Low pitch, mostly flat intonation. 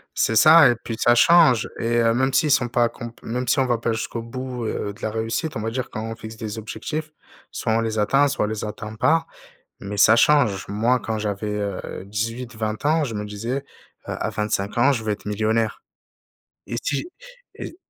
No: low, 115 Hz; average, 3.0 semitones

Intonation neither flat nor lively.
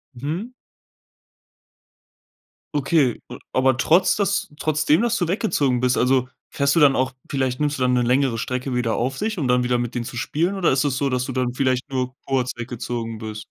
Yes: average, 3.0 semitones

